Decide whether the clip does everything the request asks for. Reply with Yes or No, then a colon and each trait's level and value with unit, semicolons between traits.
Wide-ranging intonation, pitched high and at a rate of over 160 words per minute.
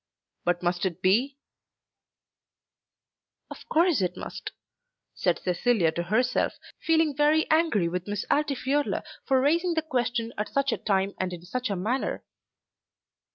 No: wide, 7.9 semitones; high, 240 Hz; average, 140 wpm